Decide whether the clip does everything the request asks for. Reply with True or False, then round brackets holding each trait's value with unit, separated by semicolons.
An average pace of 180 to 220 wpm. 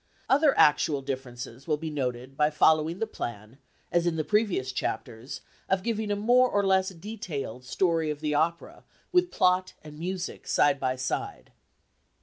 False (160 wpm)